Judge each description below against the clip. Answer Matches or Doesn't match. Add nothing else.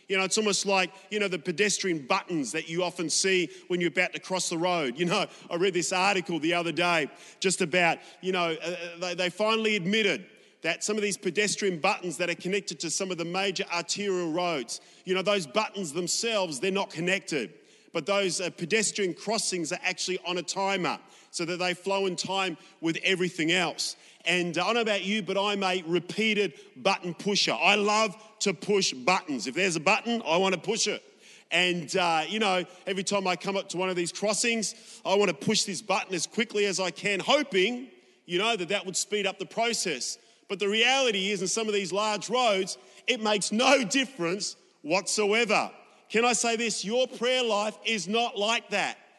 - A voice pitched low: Doesn't match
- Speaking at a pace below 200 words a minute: Doesn't match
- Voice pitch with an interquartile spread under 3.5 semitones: Matches